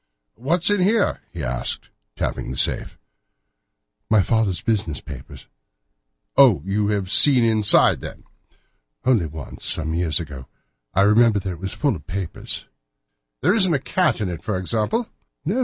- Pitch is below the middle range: Yes, low, 105 Hz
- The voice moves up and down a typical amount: No, wide, 7.1 semitones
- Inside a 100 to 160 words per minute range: Yes, average, 155 wpm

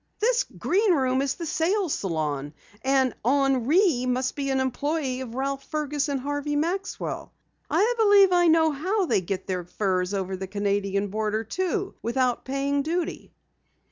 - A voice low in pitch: No, very high, 275 Hz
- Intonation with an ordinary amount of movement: No, wide, 7.2 semitones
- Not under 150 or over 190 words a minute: Yes, average, 155 wpm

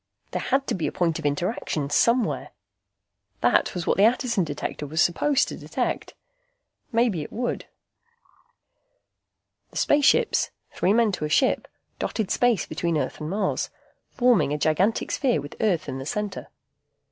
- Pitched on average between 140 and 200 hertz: Yes, high, 190 Hz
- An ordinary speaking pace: Yes, average, 155 wpm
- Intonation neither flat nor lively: No, wide, 7.3 semitones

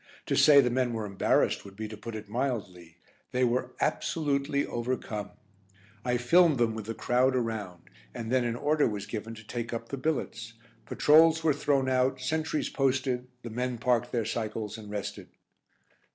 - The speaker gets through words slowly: No, average, 170 wpm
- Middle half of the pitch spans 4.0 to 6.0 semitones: No, average, 3.2 semitones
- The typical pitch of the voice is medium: No, low, 120 Hz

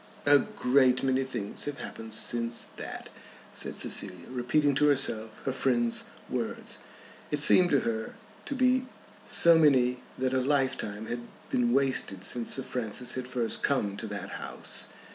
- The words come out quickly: No, average, 155 wpm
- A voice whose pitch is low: Yes, low, 125 Hz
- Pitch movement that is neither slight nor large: Yes, average, 3.4 semitones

